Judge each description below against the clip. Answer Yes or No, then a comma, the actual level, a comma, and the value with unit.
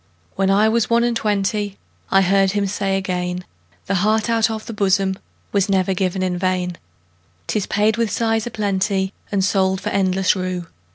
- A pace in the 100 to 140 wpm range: No, average, 155 wpm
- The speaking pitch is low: No, high, 195 Hz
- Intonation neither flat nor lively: No, narrow, 2.2 semitones